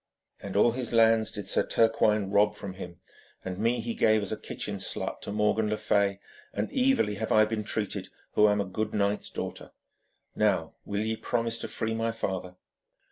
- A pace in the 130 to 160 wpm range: No, average, 190 wpm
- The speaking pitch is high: No, low, 105 Hz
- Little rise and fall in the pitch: Yes, narrow, 1.8 semitones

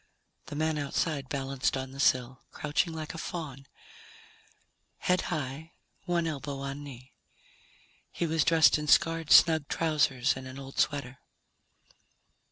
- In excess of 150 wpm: No, slow, 135 wpm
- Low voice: No, medium, 145 Hz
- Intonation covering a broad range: No, average, 3.0 semitones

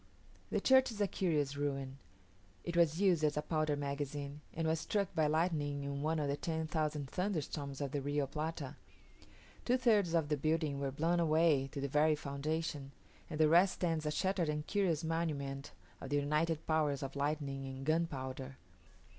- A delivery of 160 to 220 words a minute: Yes, average, 180 wpm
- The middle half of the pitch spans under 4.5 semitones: Yes, narrow, 2.6 semitones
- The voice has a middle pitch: Yes, medium, 150 Hz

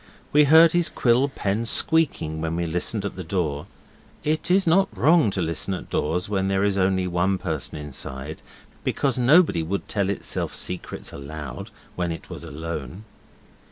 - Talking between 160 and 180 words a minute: Yes, average, 165 wpm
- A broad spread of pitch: Yes, wide, 7.6 semitones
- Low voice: Yes, very low, 95 Hz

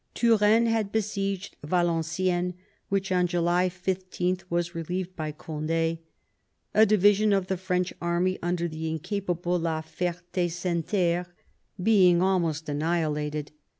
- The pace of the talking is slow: Yes, slow, 115 wpm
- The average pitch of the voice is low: No, medium, 175 Hz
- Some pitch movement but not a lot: No, narrow, 2.2 semitones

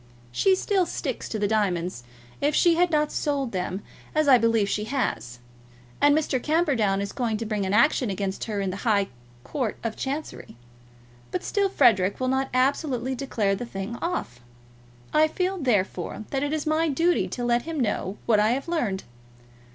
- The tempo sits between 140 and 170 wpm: No, average, 180 wpm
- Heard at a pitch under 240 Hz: No, high, 245 Hz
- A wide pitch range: Yes, wide, 6.7 semitones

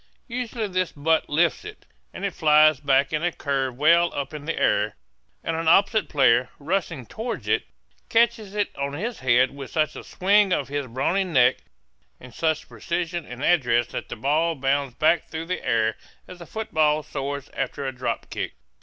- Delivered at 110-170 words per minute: No, average, 185 wpm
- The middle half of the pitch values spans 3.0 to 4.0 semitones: No, average, 4.6 semitones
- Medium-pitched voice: Yes, medium, 155 Hz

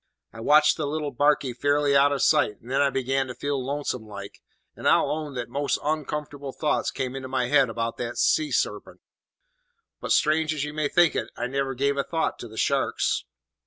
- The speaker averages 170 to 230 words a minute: Yes, fast, 205 wpm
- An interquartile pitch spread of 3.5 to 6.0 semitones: No, average, 2.7 semitones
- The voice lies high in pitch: No, medium, 140 Hz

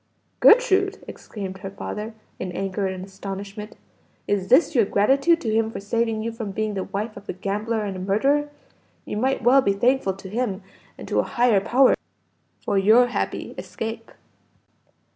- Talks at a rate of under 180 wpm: Yes, average, 165 wpm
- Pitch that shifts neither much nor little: Yes, average, 3.7 semitones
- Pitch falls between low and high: No, high, 215 Hz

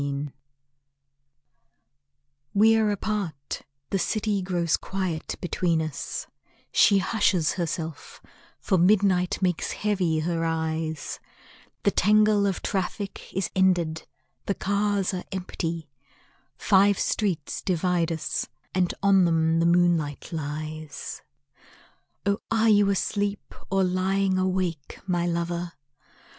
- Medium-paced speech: No, slow, 110 wpm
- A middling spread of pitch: Yes, average, 3.3 semitones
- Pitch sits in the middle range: Yes, medium, 180 Hz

